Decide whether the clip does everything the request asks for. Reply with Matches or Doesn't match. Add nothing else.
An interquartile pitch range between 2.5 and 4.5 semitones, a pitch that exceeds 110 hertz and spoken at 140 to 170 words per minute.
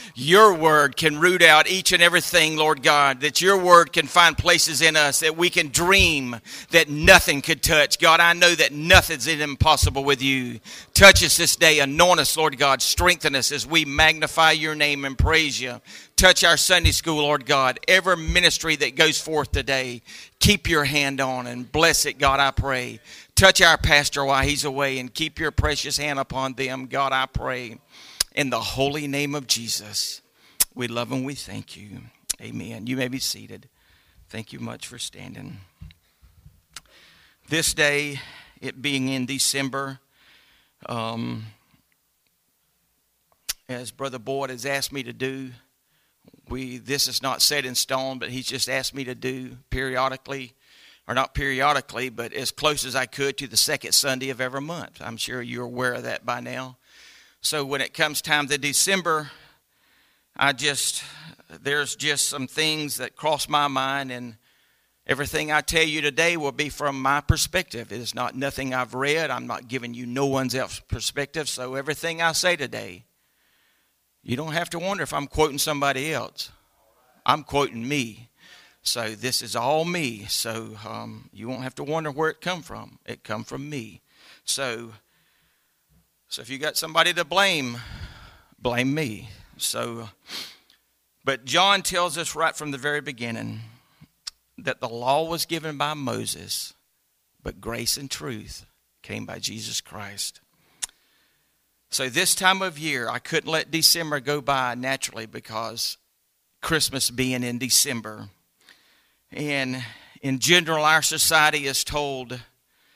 Matches